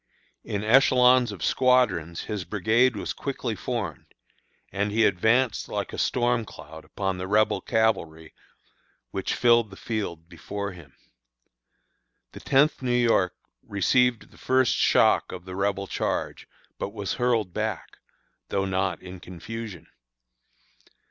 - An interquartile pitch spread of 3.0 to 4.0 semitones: No, average, 4.4 semitones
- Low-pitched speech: Yes, low, 105 Hz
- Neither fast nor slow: No, slow, 130 wpm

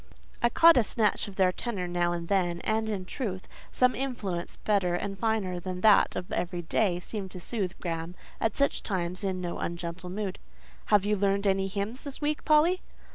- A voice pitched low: No, high, 195 Hz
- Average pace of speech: Yes, average, 190 wpm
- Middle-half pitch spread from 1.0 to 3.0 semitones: No, average, 3.6 semitones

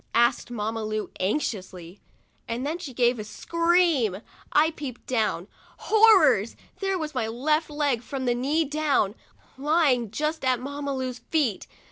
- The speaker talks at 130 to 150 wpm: Yes, average, 140 wpm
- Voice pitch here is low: No, very high, 260 Hz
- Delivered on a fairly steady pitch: No, average, 5.2 semitones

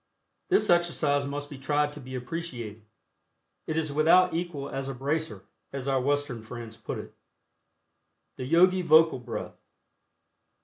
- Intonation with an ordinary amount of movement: Yes, average, 3.9 semitones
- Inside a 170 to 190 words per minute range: No, average, 140 wpm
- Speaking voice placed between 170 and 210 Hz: No, medium, 145 Hz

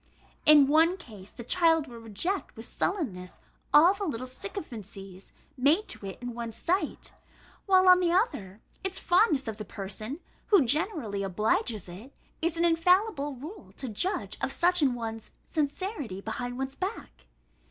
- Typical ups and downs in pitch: No, wide, 8.2 semitones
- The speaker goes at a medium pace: Yes, average, 155 wpm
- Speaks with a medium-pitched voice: No, very high, 280 Hz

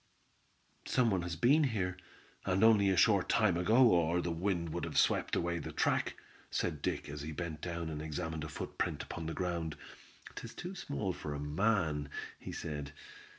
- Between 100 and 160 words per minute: No, average, 185 wpm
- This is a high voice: No, very low, 85 Hz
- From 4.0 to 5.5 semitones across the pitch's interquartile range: Yes, average, 4.4 semitones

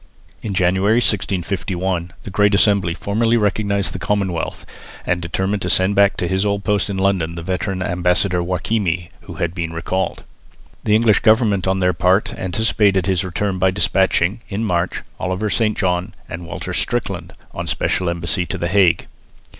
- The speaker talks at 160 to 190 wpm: Yes, average, 170 wpm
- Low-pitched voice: Yes, very low, 95 Hz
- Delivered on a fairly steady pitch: Yes, narrow, 2.3 semitones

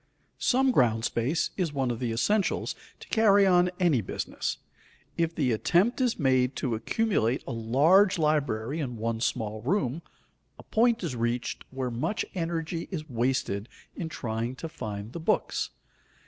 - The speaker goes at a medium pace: Yes, average, 155 wpm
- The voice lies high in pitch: No, low, 135 Hz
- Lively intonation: Yes, wide, 7.1 semitones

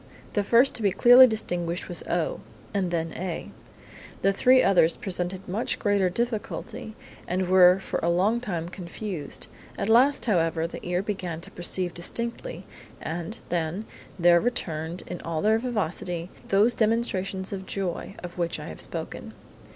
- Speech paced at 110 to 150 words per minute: No, average, 160 wpm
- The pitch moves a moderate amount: Yes, average, 4.1 semitones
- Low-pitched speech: No, high, 190 Hz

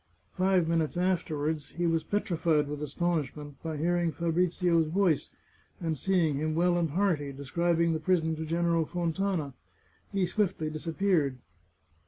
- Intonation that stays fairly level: Yes, narrow, 2.3 semitones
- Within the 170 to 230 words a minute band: No, average, 140 wpm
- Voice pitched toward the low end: No, medium, 165 Hz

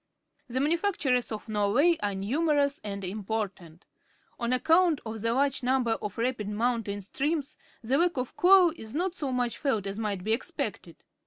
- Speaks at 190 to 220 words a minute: No, average, 170 wpm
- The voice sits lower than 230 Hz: No, high, 245 Hz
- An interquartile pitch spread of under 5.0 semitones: No, wide, 5.4 semitones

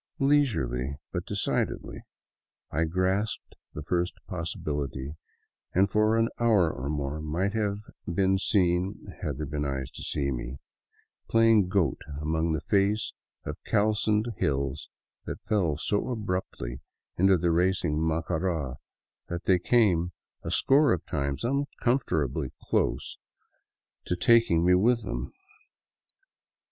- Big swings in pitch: Yes, wide, 5.9 semitones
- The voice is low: Yes, very low, 90 Hz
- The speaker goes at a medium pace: No, slow, 125 wpm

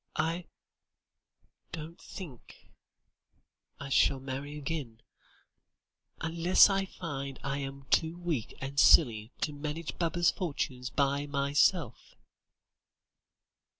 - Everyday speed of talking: No, slow, 95 wpm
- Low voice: No, medium, 145 Hz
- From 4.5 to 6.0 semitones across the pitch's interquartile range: No, average, 3.4 semitones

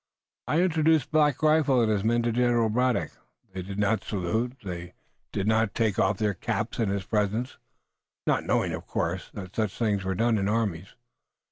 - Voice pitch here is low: Yes, low, 110 Hz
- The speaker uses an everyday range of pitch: Yes, average, 3.8 semitones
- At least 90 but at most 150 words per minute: No, average, 180 wpm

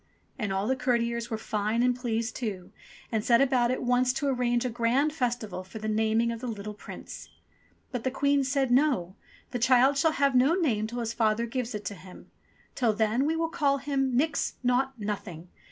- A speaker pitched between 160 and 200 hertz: No, high, 240 Hz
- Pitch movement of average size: Yes, average, 3.4 semitones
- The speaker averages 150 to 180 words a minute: No, average, 200 wpm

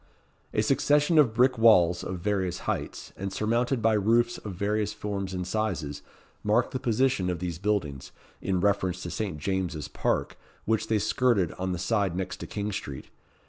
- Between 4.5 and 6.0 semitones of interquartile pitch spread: No, average, 3.5 semitones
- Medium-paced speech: Yes, average, 175 wpm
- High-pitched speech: No, low, 100 Hz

